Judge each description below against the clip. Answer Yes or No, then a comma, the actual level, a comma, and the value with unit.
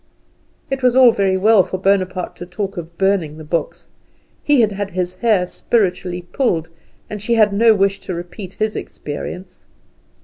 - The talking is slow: No, average, 170 wpm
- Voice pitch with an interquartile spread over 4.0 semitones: No, average, 3.1 semitones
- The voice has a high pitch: Yes, high, 195 Hz